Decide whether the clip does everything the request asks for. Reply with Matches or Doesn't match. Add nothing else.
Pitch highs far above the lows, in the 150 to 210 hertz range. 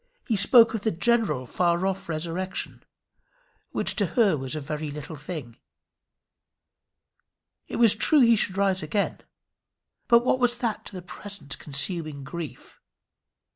Matches